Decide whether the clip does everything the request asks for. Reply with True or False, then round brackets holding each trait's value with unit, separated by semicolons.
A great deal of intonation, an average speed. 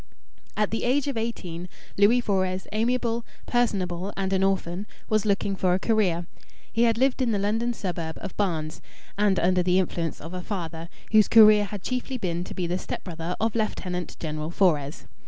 False (4.0 semitones; 180 wpm)